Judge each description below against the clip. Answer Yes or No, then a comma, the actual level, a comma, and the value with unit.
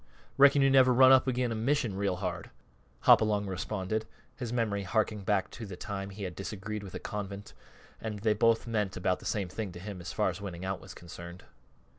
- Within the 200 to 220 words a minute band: Yes, fast, 205 wpm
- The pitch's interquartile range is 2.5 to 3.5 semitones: Yes, average, 3.1 semitones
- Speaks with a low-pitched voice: Yes, low, 105 Hz